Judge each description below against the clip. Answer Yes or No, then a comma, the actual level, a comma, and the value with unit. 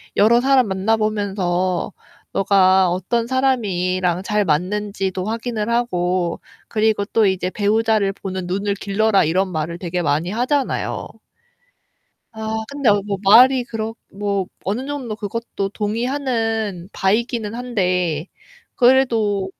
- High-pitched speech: Yes, high, 205 Hz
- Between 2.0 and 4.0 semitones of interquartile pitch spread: Yes, average, 3.6 semitones